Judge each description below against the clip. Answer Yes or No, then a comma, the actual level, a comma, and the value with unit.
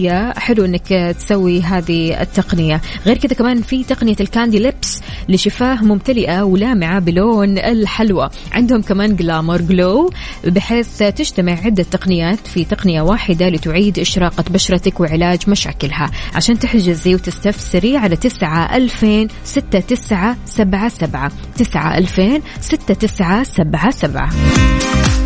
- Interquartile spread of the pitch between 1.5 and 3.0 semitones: No, average, 4.4 semitones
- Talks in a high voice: Yes, high, 195 Hz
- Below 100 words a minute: No, average, 115 wpm